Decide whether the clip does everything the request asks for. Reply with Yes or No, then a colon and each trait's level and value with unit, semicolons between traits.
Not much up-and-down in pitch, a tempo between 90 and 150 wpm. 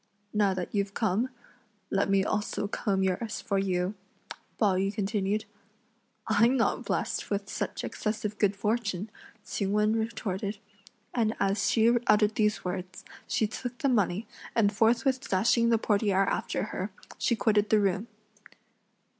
Yes: narrow, 2.2 semitones; average, 145 wpm